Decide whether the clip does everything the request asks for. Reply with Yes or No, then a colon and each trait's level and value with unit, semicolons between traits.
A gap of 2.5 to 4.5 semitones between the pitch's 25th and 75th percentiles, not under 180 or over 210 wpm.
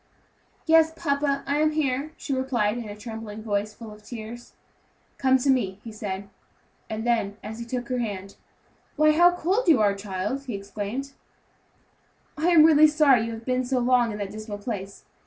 No: average, 4.9 semitones; average, 185 wpm